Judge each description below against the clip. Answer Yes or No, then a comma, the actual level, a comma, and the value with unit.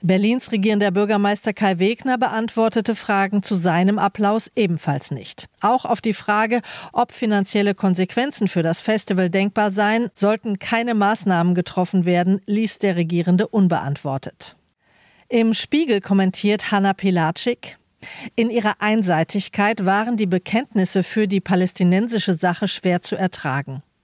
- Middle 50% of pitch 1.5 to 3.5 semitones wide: Yes, average, 2.8 semitones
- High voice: Yes, high, 200 Hz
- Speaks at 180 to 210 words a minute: No, slow, 125 wpm